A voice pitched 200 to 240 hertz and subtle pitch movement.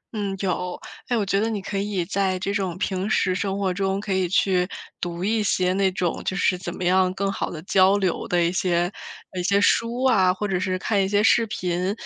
No: high, 190 Hz; narrow, 1.8 semitones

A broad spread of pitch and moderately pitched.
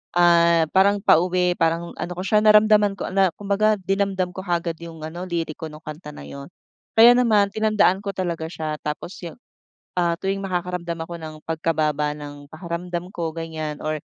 No: average, 3.3 semitones; medium, 175 Hz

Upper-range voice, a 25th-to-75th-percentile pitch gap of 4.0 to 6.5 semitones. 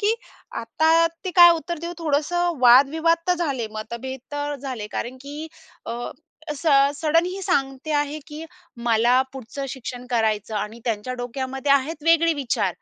Yes: very high, 280 Hz; average, 4.8 semitones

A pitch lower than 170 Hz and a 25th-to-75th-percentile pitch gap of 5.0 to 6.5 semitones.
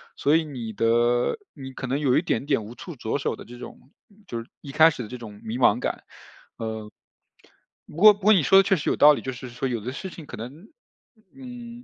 Yes: low, 135 Hz; wide, 5.6 semitones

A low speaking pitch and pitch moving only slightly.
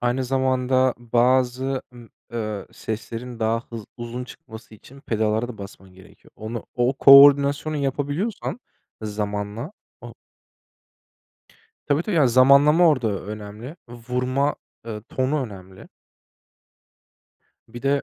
No: low, 125 Hz; average, 3.7 semitones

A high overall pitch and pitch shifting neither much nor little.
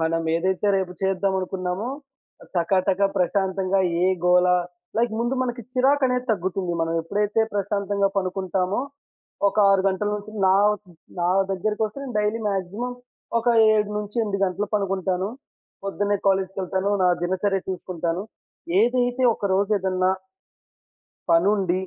No: high, 195 Hz; narrow, 2.1 semitones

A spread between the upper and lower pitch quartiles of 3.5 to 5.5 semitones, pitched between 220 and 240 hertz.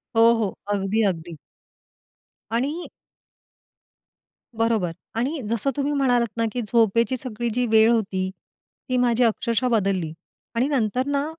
No: average, 3.1 semitones; high, 230 Hz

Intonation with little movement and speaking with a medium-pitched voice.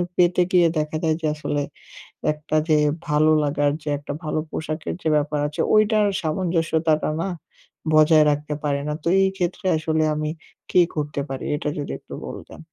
Yes: narrow, 2.0 semitones; medium, 155 Hz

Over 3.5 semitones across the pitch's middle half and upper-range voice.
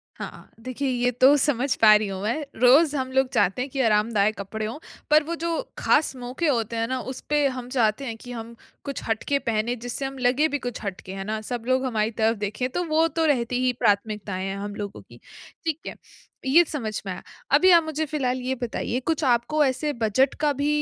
Yes: average, 4.5 semitones; very high, 250 Hz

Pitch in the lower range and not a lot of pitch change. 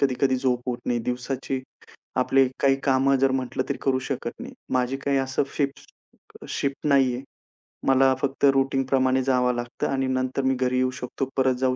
Yes: low, 130 Hz; narrow, 1.0 semitones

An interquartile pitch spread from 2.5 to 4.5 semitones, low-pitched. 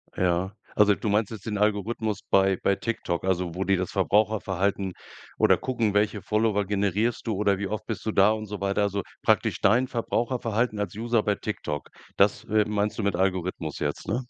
No: narrow, 2.1 semitones; low, 105 Hz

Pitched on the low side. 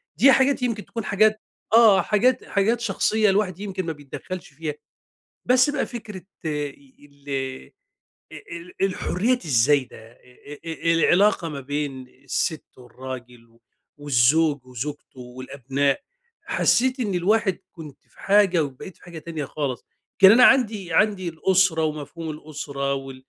No: medium, 165 Hz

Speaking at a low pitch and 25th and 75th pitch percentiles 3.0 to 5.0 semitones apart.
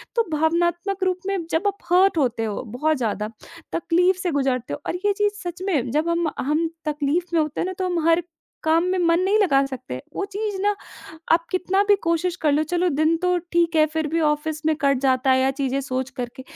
No: very high, 320 Hz; average, 4.6 semitones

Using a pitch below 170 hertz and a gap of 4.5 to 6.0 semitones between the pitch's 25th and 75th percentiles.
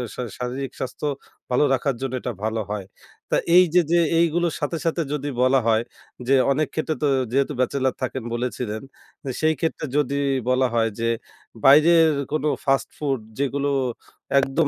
No: low, 135 Hz; average, 3.3 semitones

